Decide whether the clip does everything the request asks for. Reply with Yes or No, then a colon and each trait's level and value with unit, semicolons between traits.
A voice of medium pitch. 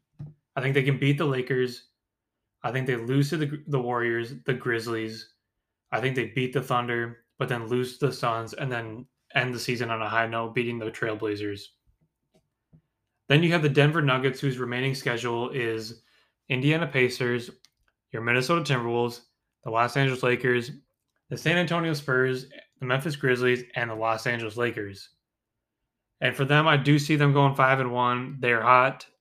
No: low, 125 Hz